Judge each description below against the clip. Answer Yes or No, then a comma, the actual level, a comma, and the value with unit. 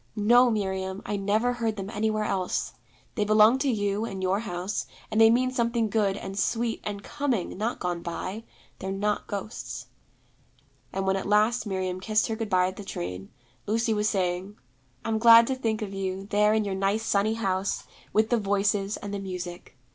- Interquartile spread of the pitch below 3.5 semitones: Yes, narrow, 2.6 semitones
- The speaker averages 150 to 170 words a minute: No, average, 190 wpm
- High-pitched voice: Yes, high, 205 Hz